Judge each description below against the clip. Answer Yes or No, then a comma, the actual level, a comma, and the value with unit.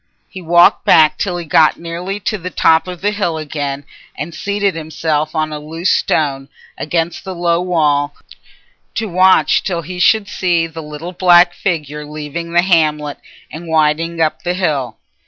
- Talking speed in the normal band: Yes, average, 170 wpm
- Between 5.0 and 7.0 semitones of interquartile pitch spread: No, average, 2.8 semitones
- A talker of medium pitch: Yes, medium, 165 Hz